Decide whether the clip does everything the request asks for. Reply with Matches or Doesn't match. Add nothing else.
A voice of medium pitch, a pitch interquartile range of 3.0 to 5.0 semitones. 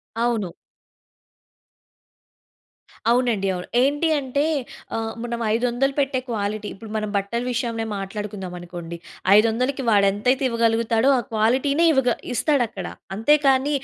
Doesn't match